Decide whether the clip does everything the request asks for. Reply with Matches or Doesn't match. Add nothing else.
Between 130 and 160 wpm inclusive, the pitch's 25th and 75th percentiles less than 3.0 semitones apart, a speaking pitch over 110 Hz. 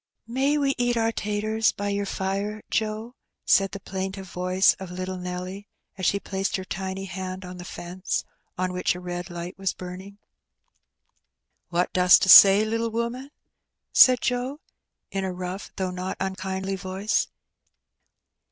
Matches